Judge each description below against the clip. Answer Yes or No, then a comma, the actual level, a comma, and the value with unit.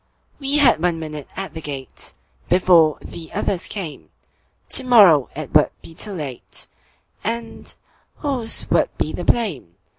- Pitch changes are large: Yes, wide, 6.8 semitones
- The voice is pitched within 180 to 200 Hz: No, medium, 170 Hz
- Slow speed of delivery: Yes, slow, 125 wpm